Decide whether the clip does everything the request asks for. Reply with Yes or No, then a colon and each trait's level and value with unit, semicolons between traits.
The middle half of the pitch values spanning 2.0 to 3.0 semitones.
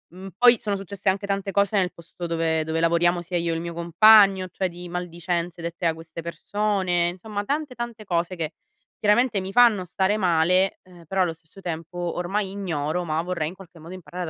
Yes: average, 2.7 semitones